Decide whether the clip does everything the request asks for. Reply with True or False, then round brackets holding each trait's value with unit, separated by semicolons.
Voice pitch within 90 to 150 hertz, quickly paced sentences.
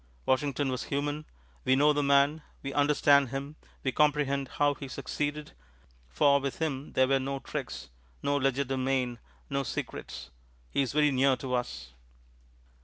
False (140 Hz; 150 wpm)